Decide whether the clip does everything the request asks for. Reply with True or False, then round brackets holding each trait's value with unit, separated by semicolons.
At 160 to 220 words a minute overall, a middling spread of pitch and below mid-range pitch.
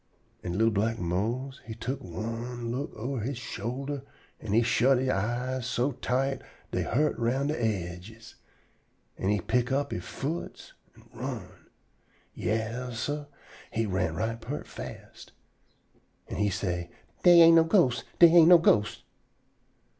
False (145 wpm; 4.0 semitones; 120 Hz)